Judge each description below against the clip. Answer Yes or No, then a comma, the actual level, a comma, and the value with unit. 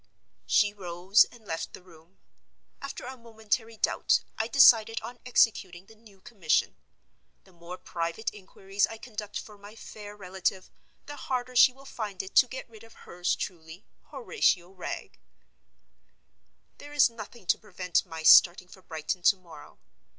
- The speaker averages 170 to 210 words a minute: No, average, 155 wpm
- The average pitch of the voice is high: Yes, high, 205 Hz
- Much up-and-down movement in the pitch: No, average, 4.1 semitones